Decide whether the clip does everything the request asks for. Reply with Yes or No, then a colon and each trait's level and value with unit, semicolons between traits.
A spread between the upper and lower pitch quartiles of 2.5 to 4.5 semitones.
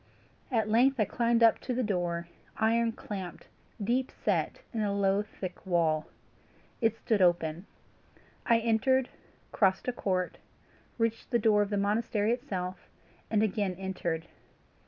Yes: average, 3.6 semitones